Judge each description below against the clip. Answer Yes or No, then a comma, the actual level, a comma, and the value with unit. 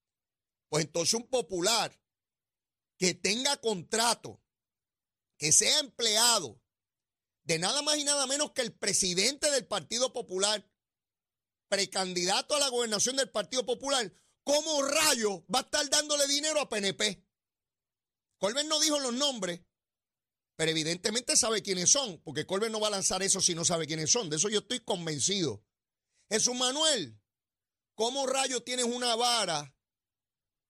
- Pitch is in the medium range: No, high, 210 Hz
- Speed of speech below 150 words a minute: Yes, average, 140 wpm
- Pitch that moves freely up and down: Yes, wide, 8.0 semitones